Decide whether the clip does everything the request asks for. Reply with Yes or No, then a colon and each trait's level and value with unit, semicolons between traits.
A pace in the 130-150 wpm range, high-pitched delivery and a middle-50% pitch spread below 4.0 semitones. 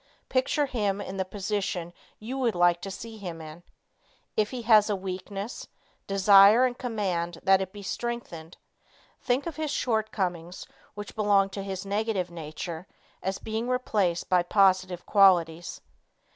Yes: average, 145 wpm; high, 195 Hz; average, 3.4 semitones